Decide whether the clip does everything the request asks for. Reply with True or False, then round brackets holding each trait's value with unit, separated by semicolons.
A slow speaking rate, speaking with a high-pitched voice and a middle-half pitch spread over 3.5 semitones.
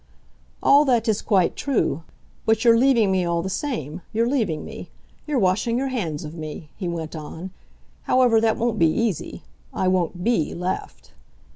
False (170 wpm; 195 Hz; 5.6 semitones)